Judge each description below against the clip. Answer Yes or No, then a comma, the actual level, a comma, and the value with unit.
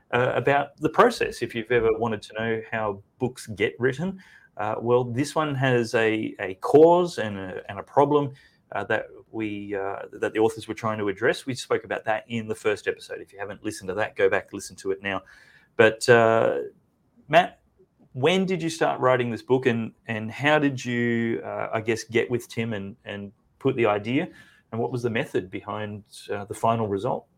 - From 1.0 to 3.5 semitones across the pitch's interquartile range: No, average, 4.4 semitones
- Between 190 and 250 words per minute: Yes, fast, 205 wpm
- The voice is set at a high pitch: No, low, 120 Hz